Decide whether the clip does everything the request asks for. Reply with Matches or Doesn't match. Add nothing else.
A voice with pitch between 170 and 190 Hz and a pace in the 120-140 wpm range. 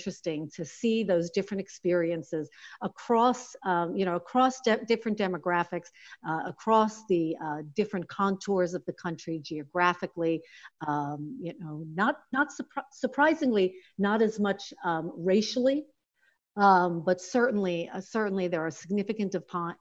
Matches